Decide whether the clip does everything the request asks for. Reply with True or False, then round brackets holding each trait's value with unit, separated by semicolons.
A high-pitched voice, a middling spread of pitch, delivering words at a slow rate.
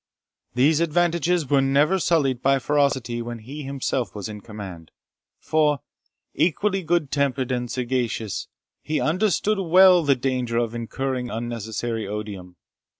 False (135 Hz; 4.9 semitones; 130 wpm)